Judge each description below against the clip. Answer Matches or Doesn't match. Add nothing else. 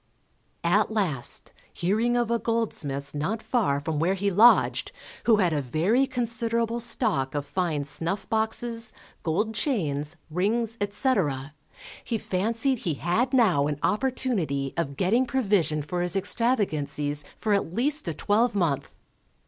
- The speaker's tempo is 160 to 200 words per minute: Doesn't match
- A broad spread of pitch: Matches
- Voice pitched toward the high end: Matches